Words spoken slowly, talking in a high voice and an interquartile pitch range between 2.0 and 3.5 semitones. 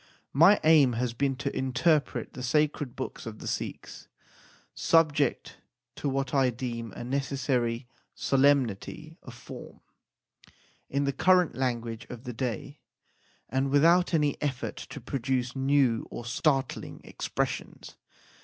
No: slow, 125 wpm; low, 135 Hz; average, 2.9 semitones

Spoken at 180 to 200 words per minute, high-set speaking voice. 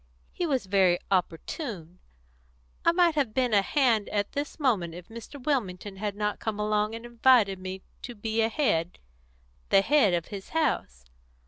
No: average, 165 wpm; high, 215 Hz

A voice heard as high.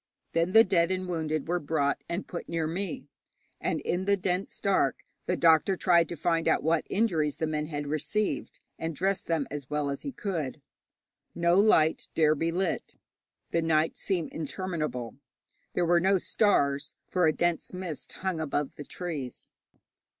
No: medium, 165 Hz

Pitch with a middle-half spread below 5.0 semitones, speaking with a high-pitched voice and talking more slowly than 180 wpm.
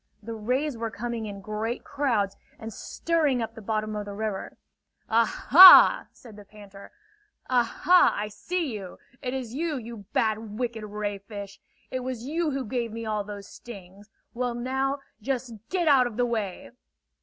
Yes: average, 3.5 semitones; high, 230 Hz; average, 170 wpm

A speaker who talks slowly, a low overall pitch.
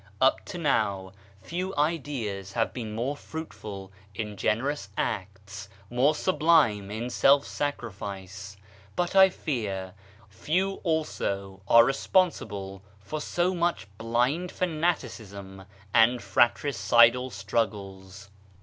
Yes: slow, 105 wpm; low, 115 Hz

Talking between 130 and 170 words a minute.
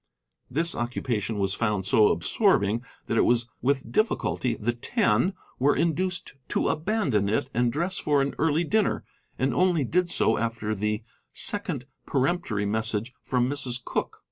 Yes: average, 150 wpm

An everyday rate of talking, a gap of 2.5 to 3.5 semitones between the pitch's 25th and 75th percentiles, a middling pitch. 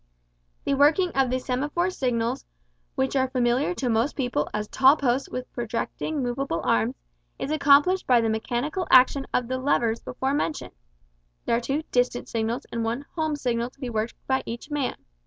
No: average, 175 wpm; average, 3.2 semitones; very high, 255 Hz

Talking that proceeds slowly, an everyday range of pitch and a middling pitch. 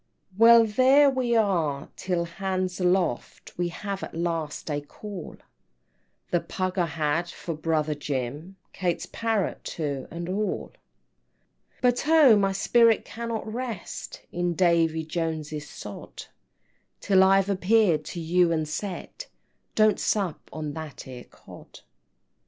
Yes: slow, 130 wpm; average, 4.7 semitones; medium, 180 Hz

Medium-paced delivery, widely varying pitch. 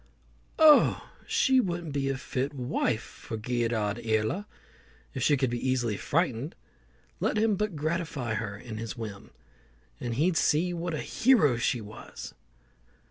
Yes: average, 145 wpm; wide, 6.8 semitones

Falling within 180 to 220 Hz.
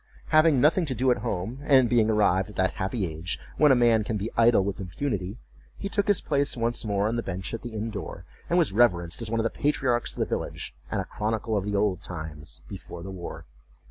No: low, 110 Hz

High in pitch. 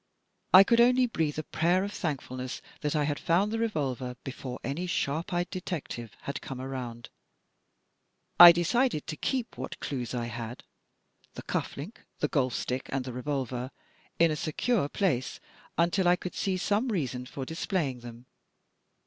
No: medium, 150 Hz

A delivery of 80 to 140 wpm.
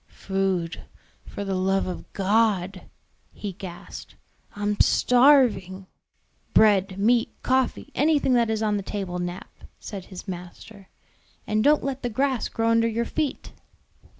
Yes: slow, 135 wpm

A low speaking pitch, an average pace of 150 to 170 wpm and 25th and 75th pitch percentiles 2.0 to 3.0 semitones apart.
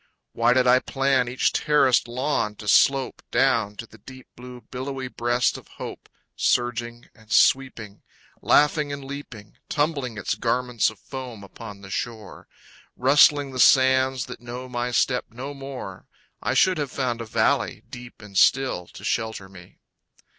Yes: low, 125 Hz; average, 155 wpm; average, 2.7 semitones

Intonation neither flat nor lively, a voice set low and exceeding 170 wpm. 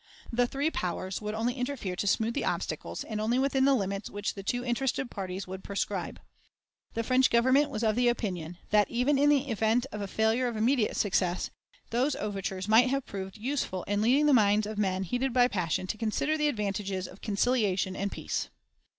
No: average, 4.2 semitones; high, 220 Hz; average, 200 wpm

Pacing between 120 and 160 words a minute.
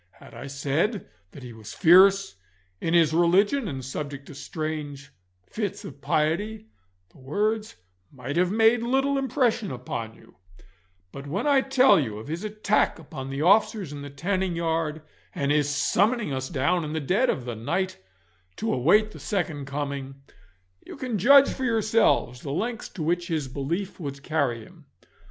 No: average, 170 wpm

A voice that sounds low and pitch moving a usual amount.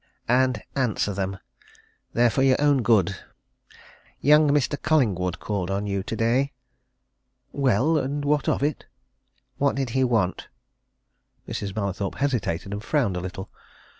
No: low, 120 Hz; wide, 6.0 semitones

